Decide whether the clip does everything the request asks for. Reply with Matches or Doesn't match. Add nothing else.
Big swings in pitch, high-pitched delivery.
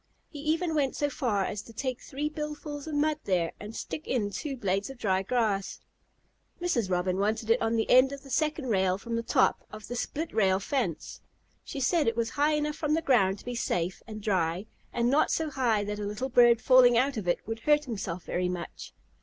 Matches